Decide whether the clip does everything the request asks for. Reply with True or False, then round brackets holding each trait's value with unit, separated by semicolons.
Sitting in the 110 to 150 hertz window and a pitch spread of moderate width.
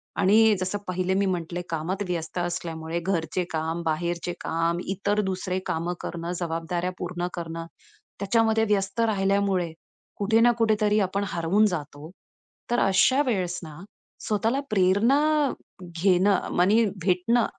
False (185 Hz; 3.1 semitones)